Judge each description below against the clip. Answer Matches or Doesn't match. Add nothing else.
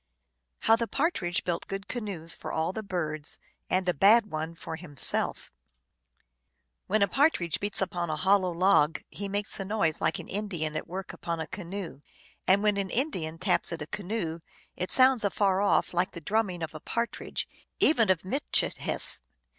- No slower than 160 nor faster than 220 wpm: Matches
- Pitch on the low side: Doesn't match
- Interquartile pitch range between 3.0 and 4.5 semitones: Matches